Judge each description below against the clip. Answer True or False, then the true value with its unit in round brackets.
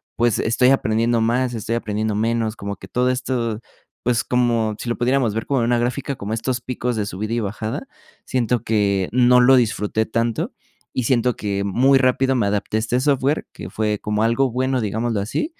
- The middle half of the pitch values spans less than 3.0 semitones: True (2.6 semitones)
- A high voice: False (115 Hz)